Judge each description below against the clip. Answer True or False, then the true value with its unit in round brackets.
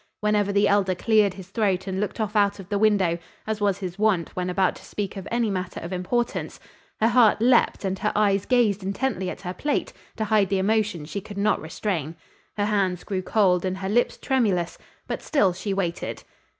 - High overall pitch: True (200 Hz)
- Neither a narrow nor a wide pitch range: False (2.3 semitones)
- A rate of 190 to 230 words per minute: True (205 wpm)